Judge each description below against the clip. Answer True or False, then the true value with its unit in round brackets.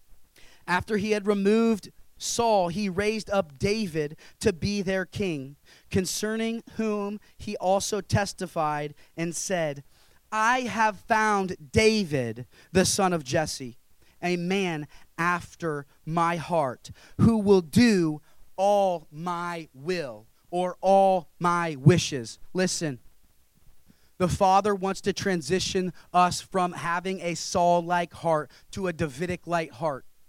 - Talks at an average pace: False (115 wpm)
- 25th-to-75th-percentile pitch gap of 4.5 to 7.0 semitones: False (3.7 semitones)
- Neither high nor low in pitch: True (180 Hz)